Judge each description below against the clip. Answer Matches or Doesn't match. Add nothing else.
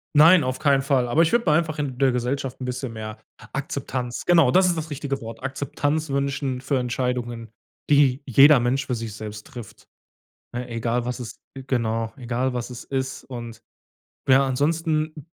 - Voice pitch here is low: Matches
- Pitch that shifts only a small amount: Doesn't match